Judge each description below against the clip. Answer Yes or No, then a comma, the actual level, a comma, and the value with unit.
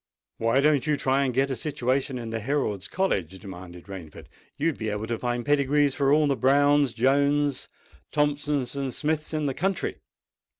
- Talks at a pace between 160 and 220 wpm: Yes, average, 180 wpm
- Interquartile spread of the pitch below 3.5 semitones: No, average, 3.9 semitones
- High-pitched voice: No, low, 135 Hz